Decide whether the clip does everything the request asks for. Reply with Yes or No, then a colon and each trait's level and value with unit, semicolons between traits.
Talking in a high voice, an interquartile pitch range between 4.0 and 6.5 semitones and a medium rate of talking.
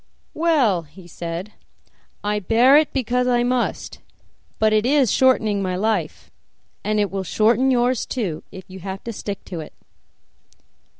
Yes: high, 215 Hz; average, 4.7 semitones; average, 155 wpm